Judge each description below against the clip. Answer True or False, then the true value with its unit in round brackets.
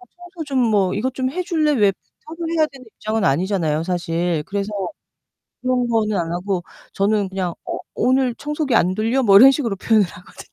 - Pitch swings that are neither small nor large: False (6.2 semitones)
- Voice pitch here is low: False (215 Hz)